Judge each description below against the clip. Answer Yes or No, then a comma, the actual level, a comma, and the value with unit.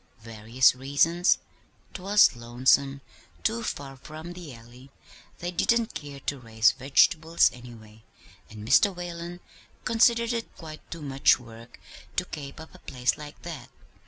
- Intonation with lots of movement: Yes, wide, 6.0 semitones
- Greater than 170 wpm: No, average, 140 wpm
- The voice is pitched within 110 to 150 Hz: Yes, medium, 140 Hz